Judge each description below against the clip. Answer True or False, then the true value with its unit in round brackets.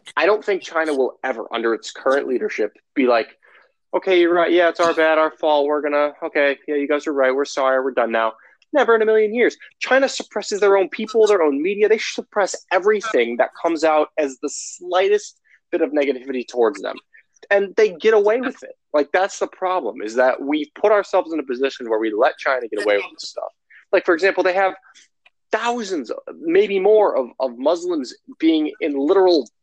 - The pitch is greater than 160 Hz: True (185 Hz)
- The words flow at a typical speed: False (210 wpm)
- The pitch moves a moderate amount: False (7.1 semitones)